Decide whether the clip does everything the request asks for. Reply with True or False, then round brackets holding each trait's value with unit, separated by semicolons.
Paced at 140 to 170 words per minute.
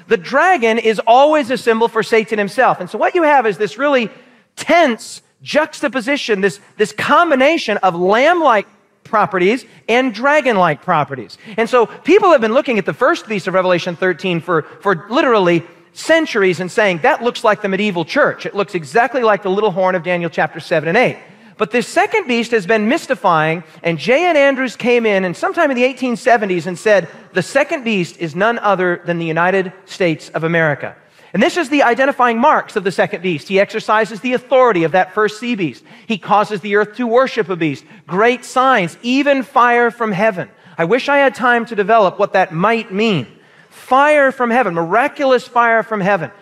False (195 wpm)